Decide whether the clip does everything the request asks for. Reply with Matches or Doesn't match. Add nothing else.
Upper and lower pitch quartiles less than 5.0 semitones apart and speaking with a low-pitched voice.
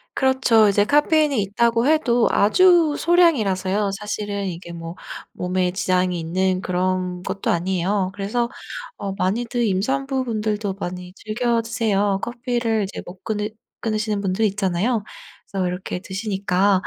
Doesn't match